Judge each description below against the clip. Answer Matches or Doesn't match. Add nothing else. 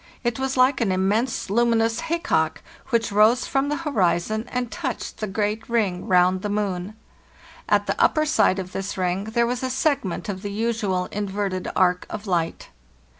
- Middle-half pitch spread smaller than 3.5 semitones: Doesn't match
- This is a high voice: Matches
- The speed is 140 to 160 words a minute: Doesn't match